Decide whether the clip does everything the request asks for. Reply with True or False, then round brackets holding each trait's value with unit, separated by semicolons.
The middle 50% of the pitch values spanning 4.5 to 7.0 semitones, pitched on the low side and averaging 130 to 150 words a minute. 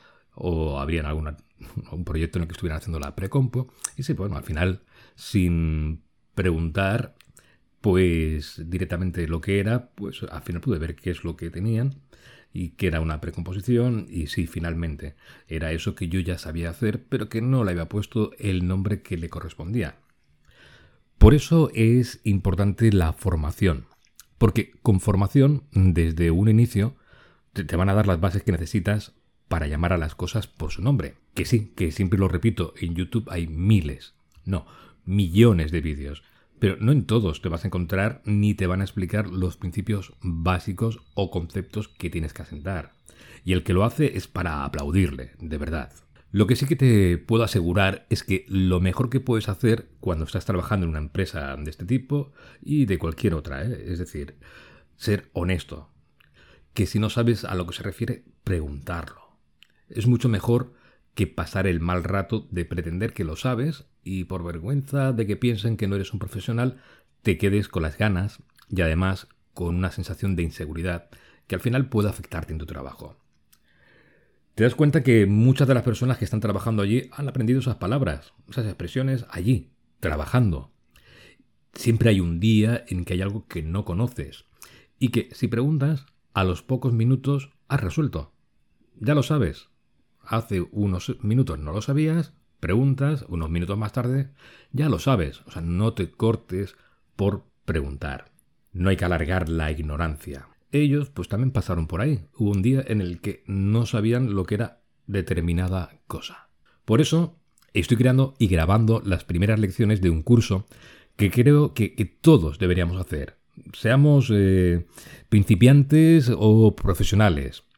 False (5.3 semitones; 100 Hz; 170 wpm)